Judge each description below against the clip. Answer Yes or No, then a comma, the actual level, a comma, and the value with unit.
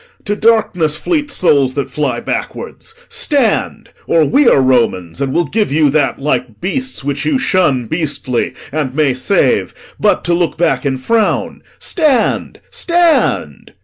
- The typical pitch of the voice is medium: Yes, medium, 155 Hz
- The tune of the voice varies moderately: No, wide, 9.0 semitones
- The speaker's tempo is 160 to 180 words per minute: No, average, 145 wpm